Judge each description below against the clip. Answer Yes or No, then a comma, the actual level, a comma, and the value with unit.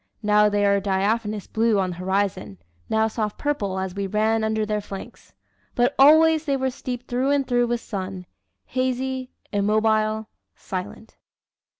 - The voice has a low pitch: No, high, 215 Hz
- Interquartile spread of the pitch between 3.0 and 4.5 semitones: Yes, average, 3.9 semitones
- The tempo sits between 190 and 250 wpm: No, average, 155 wpm